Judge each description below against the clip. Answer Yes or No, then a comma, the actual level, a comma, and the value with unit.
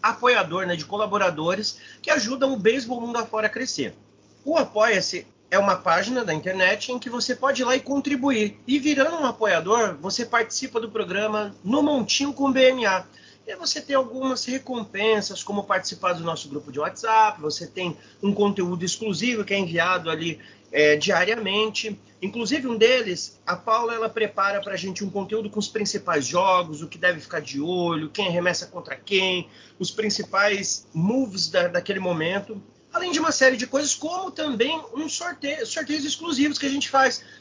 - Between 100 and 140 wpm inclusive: No, average, 175 wpm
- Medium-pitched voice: No, high, 215 Hz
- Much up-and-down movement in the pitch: Yes, wide, 6.1 semitones